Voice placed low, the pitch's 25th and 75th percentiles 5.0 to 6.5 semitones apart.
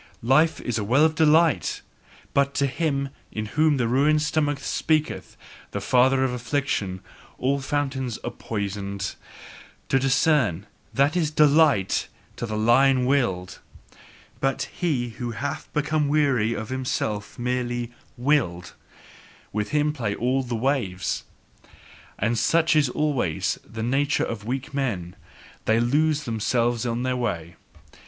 No: low, 130 Hz; average, 4.5 semitones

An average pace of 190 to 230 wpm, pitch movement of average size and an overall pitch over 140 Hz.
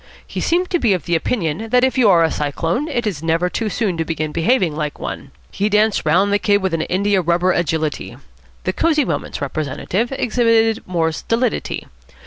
No: average, 195 wpm; wide, 5.7 semitones; medium, 185 Hz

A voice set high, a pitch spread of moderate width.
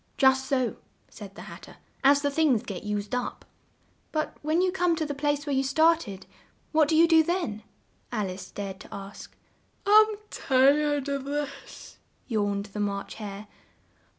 No: very high, 275 Hz; wide, 6.8 semitones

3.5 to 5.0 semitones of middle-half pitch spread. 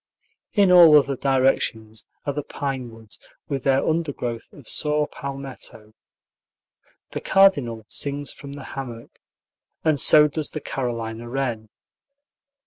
Yes: average, 3.9 semitones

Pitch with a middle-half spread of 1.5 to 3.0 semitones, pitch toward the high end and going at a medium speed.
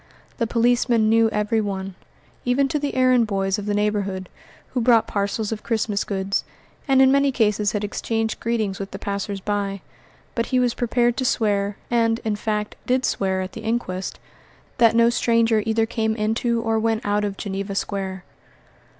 Yes: narrow, 2.5 semitones; high, 220 Hz; average, 175 wpm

